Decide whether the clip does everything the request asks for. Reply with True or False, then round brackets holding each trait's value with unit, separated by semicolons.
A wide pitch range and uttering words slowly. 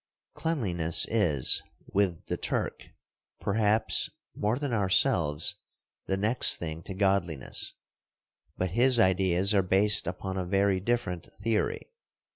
False (3.1 semitones; 115 wpm)